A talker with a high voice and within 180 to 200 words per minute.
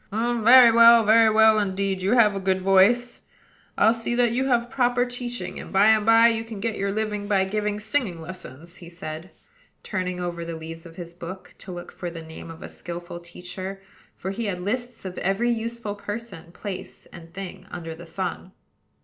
Yes: high, 195 Hz; average, 195 wpm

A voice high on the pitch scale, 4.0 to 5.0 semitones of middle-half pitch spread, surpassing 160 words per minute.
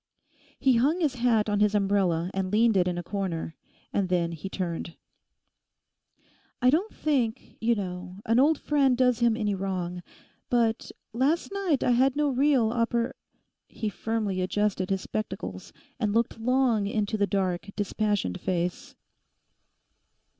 No: high, 215 Hz; average, 4.7 semitones; average, 145 wpm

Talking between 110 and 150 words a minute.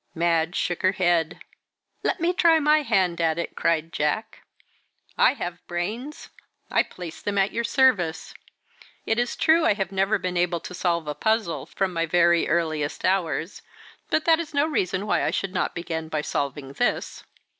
No: average, 175 wpm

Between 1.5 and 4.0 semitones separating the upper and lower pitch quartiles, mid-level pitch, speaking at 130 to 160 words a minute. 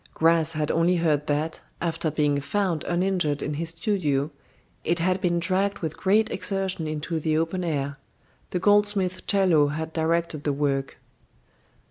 Yes: average, 3.6 semitones; medium, 165 Hz; average, 150 wpm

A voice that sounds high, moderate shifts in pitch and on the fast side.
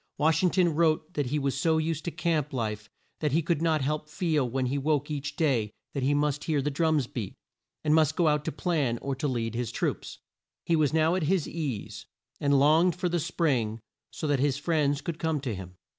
No: medium, 150 Hz; average, 3.0 semitones; fast, 225 wpm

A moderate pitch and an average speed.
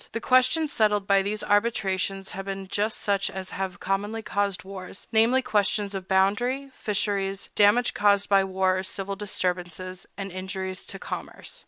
No: high, 195 Hz; average, 160 wpm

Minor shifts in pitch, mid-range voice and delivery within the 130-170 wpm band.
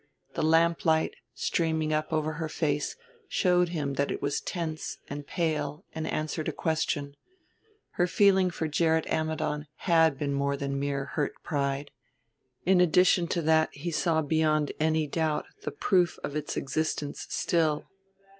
Yes: narrow, 2.2 semitones; medium, 155 Hz; average, 155 wpm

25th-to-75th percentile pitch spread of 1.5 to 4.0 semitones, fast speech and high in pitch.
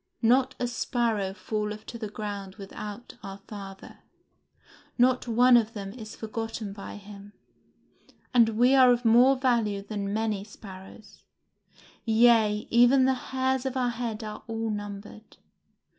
No: average, 2.9 semitones; average, 140 wpm; high, 220 Hz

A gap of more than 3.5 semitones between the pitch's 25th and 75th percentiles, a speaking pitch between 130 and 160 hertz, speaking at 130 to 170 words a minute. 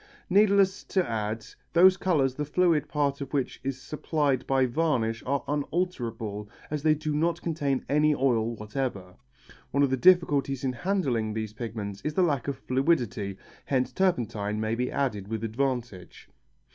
Yes: average, 5.2 semitones; low, 135 Hz; average, 160 wpm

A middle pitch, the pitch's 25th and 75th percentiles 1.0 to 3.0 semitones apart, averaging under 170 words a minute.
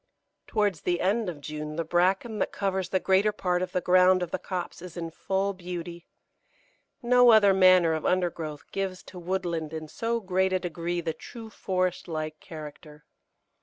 No: medium, 180 Hz; narrow, 2.4 semitones; average, 175 wpm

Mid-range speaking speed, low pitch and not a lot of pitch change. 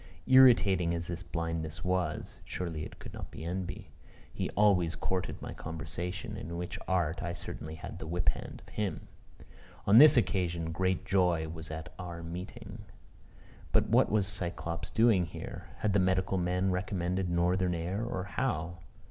Yes: average, 160 wpm; very low, 90 Hz; narrow, 2.1 semitones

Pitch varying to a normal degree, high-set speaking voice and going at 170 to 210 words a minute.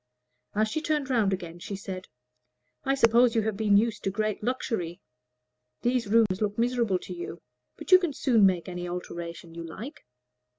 Yes: average, 4.8 semitones; high, 215 Hz; average, 175 wpm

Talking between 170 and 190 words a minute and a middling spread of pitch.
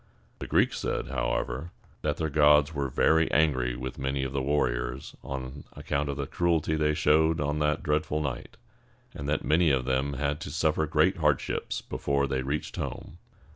No: average, 175 wpm; narrow, 2.3 semitones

